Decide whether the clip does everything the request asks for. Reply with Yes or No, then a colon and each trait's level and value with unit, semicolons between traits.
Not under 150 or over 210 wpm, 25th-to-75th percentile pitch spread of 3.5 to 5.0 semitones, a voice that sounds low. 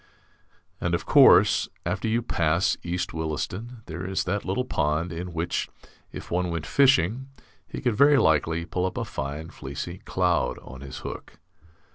Yes: average, 160 wpm; average, 4.3 semitones; very low, 90 Hz